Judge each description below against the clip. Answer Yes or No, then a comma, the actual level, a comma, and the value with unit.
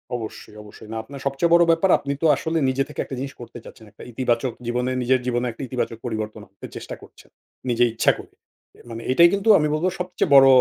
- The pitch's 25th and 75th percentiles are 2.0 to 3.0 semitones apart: No, average, 4.5 semitones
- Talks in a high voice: No, low, 130 Hz